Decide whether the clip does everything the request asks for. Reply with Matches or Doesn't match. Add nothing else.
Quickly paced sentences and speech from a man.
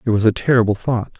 Matches